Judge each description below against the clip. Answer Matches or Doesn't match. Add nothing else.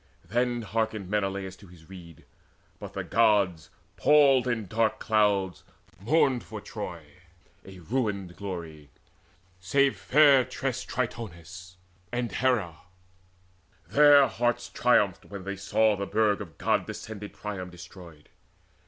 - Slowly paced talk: Matches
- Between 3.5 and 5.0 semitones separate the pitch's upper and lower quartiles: Matches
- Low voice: Matches